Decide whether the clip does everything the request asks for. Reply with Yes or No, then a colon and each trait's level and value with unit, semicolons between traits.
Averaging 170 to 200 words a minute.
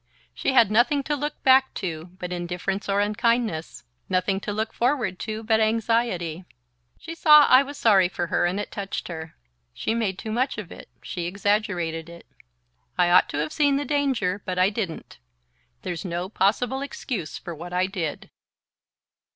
Yes: average, 175 wpm